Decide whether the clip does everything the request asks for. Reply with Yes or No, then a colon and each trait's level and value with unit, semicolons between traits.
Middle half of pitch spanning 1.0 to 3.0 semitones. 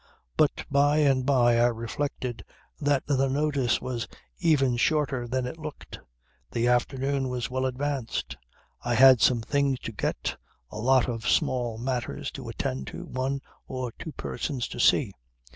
Yes: narrow, 2.6 semitones